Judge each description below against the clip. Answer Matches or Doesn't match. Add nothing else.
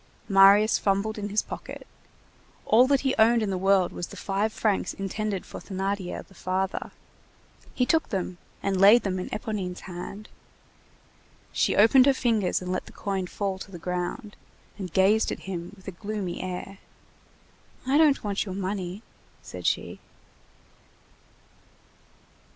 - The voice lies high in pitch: Matches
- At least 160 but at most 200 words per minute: Doesn't match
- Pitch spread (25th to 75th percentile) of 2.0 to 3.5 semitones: Matches